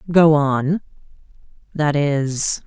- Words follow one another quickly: No, slow, 70 wpm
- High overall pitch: No, medium, 150 Hz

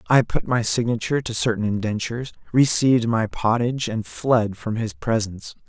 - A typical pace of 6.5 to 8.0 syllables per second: No, 5.4 syllables/s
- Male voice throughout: Yes, male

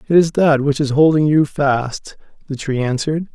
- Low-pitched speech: No, medium, 145 Hz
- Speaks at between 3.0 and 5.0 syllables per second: Yes, 4.9 syllables/s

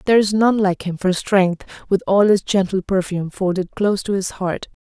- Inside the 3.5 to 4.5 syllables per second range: No, 5.3 syllables/s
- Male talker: No, female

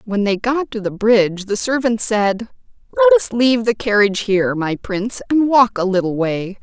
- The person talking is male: No, female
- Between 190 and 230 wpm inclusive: Yes, average, 200 wpm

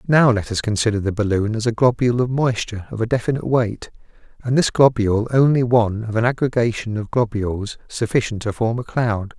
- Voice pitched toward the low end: Yes, low, 115 Hz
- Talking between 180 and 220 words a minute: Yes, average, 190 wpm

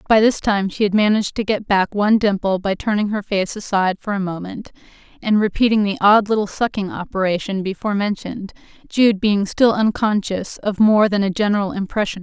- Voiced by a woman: Yes, female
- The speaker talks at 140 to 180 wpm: No, average, 200 wpm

